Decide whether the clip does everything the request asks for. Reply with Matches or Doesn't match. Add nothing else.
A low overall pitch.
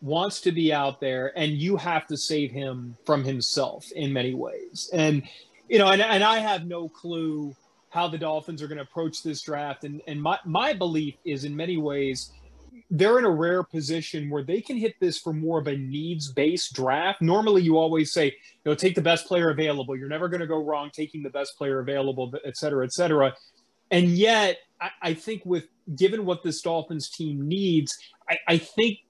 Doesn't match